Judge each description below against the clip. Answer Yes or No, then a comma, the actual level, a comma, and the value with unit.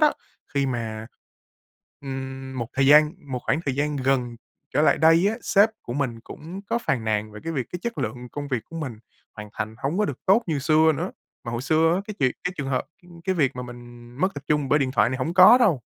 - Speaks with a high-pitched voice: No, medium, 140 Hz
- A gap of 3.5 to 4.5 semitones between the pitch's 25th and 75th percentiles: No, average, 4.9 semitones